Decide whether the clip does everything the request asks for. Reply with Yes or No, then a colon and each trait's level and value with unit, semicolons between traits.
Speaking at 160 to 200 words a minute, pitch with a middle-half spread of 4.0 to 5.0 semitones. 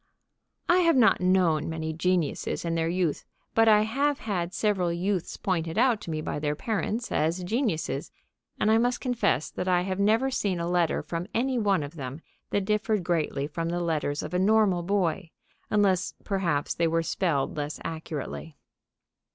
Yes: average, 175 wpm; average, 4.5 semitones